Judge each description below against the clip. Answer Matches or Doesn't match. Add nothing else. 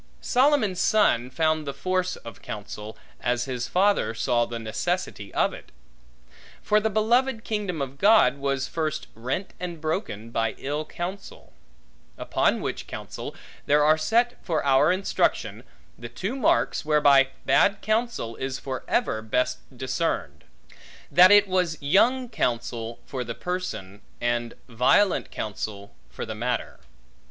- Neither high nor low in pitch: Matches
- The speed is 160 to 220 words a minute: Doesn't match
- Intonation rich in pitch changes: Matches